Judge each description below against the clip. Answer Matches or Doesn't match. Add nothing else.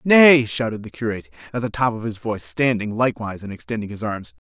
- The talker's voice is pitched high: Doesn't match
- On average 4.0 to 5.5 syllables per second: Doesn't match